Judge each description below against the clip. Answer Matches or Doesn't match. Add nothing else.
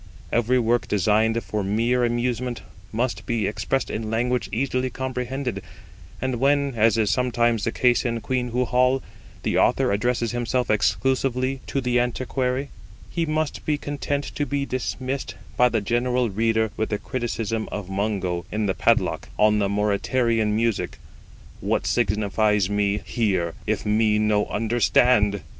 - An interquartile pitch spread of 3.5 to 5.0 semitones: Doesn't match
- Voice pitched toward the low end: Matches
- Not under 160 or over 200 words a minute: Doesn't match